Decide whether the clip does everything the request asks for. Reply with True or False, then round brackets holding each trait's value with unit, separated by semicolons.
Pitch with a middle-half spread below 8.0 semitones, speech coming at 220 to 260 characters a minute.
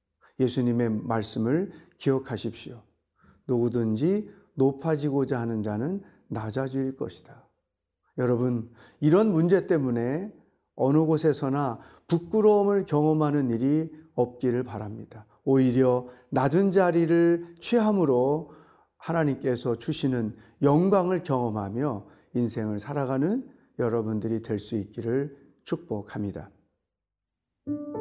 True (5.5 semitones; 245 characters per minute)